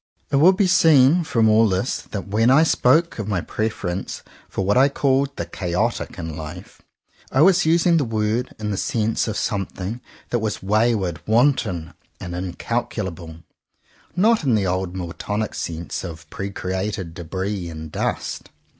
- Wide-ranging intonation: Yes, wide, 5.7 semitones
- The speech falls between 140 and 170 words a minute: Yes, average, 160 wpm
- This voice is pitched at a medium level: No, low, 105 Hz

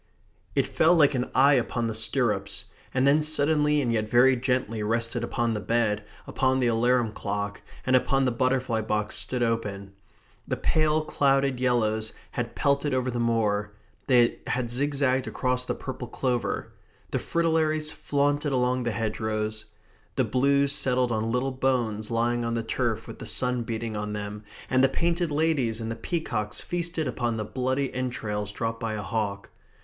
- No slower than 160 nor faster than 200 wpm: Yes, average, 165 wpm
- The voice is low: Yes, low, 125 Hz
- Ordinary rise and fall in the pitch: Yes, average, 3.3 semitones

